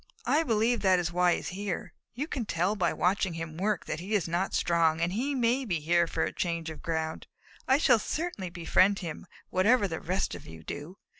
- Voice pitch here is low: No, medium, 185 Hz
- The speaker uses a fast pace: Yes, fast, 220 wpm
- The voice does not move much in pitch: No, average, 4.4 semitones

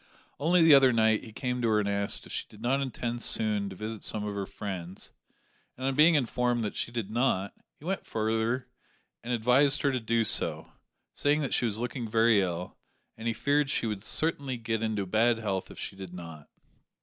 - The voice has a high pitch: No, low, 115 Hz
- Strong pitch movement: No, average, 3.7 semitones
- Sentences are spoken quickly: Yes, fast, 210 wpm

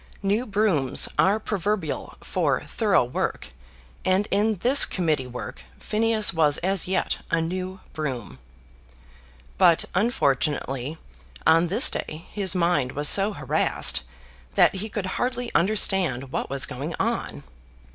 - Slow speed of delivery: Yes, slow, 125 wpm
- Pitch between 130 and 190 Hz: Yes, medium, 185 Hz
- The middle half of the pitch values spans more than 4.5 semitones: Yes, wide, 5.6 semitones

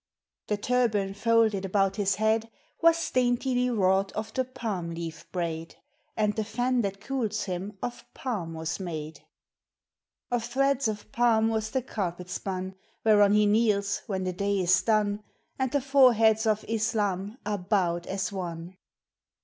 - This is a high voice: Yes, high, 210 Hz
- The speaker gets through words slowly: No, average, 150 wpm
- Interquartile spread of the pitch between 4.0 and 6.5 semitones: No, average, 3.4 semitones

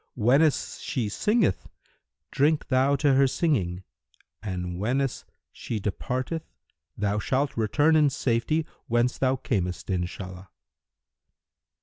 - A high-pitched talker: No, low, 125 Hz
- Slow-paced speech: Yes, slow, 105 wpm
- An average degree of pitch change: No, wide, 5.9 semitones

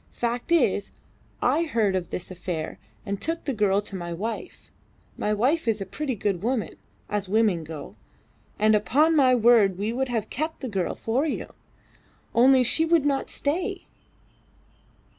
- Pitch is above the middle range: Yes, high, 225 Hz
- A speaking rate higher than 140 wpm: Yes, average, 160 wpm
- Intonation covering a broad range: Yes, wide, 5.9 semitones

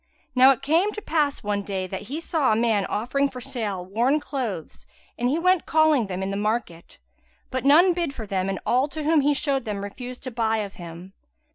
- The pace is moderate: No, fast, 220 wpm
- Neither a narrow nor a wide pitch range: No, wide, 6.2 semitones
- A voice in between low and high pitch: No, high, 245 Hz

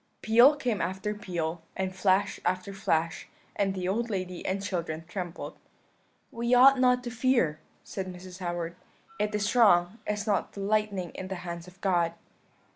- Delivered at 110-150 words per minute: No, average, 165 wpm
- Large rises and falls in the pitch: No, average, 3.2 semitones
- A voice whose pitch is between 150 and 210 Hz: Yes, high, 190 Hz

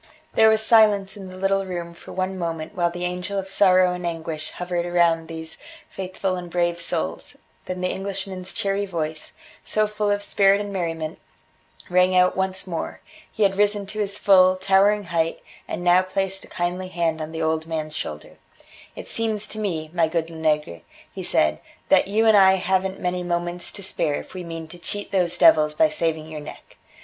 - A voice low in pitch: No, medium, 180 Hz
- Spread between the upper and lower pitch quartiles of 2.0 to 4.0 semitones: Yes, average, 2.8 semitones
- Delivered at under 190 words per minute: No, average, 195 wpm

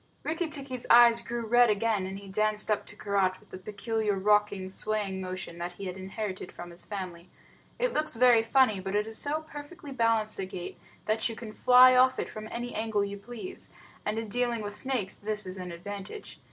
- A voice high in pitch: Yes, high, 215 Hz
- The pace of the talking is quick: Yes, fast, 210 wpm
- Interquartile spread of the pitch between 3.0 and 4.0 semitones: Yes, average, 3.7 semitones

